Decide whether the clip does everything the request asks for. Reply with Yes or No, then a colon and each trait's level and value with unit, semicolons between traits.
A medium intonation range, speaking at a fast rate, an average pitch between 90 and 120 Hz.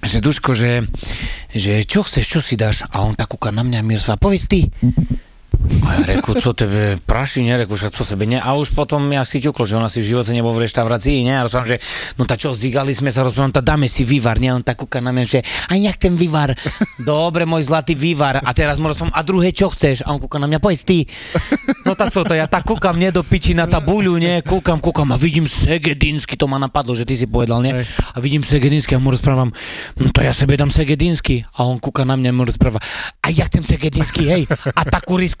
No: average, 4.4 semitones; fast, 235 wpm; low, 135 Hz